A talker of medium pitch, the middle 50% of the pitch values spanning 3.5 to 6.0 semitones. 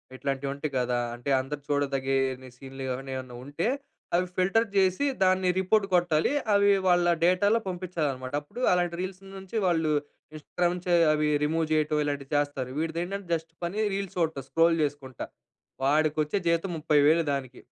Yes: medium, 155 Hz; average, 4.6 semitones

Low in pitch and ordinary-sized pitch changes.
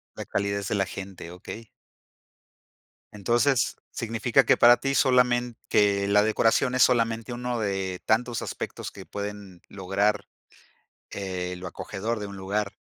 Yes: low, 105 Hz; average, 3.3 semitones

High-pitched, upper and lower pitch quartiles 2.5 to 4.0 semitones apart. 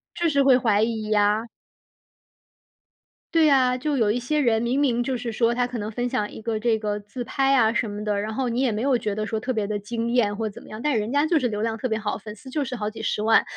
Yes: high, 230 Hz; average, 3.0 semitones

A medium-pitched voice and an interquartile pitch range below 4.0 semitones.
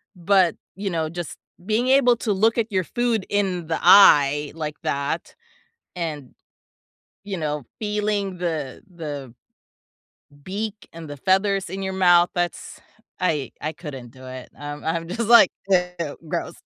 No: medium, 175 Hz; average, 4.9 semitones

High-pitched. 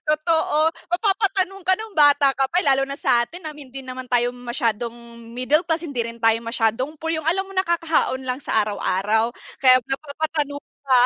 Yes: very high, 280 Hz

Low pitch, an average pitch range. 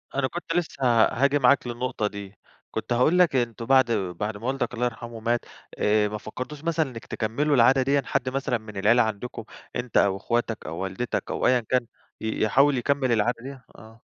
Yes: low, 120 Hz; average, 3.3 semitones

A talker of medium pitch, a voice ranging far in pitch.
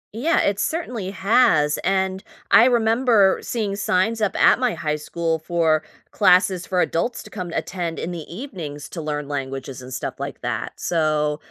Yes: medium, 180 Hz; wide, 5.7 semitones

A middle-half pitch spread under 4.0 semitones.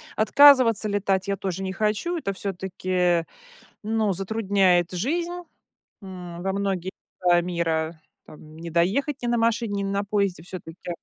Yes: average, 3.4 semitones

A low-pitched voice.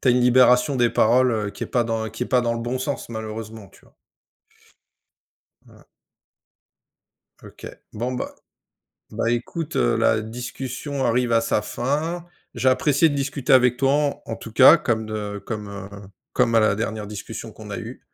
Yes: low, 120 Hz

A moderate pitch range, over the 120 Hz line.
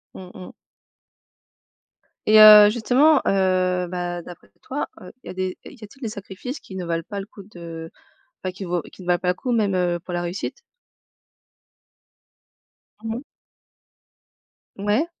Yes: average, 3.2 semitones; high, 190 Hz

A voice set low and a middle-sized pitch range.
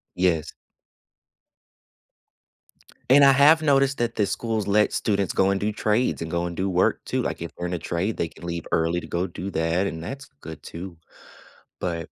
Yes: very low, 95 Hz; average, 4.5 semitones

